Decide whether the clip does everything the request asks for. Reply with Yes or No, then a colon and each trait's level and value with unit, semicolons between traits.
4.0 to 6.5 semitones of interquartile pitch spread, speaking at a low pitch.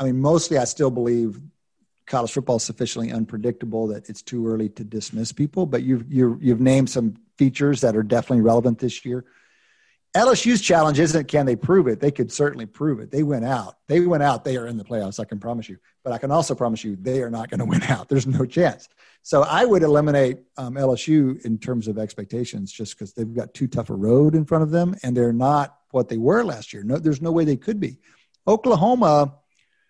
Yes: average, 4.4 semitones; low, 130 Hz